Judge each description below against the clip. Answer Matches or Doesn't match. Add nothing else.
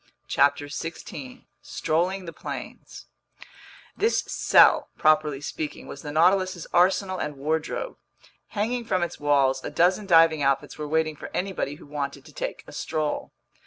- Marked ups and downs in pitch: Doesn't match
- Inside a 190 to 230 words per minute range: Doesn't match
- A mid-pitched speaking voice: Matches